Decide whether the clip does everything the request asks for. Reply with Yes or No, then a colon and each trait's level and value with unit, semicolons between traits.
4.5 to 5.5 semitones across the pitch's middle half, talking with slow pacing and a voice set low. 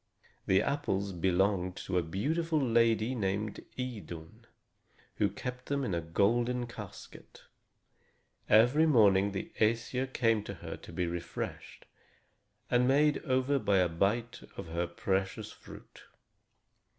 Yes: average, 4.9 semitones; slow, 125 wpm; low, 110 Hz